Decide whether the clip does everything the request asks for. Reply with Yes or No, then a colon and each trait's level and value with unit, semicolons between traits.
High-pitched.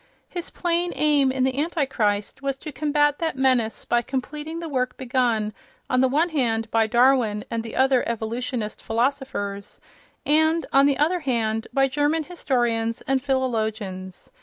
Yes: very high, 260 Hz